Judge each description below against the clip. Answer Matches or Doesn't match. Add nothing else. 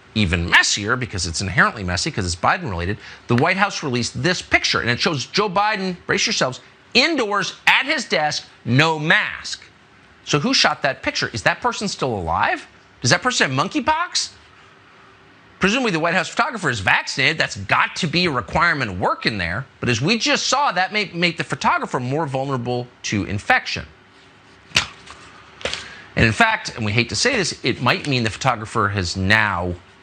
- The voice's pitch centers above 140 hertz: Doesn't match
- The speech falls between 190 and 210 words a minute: Doesn't match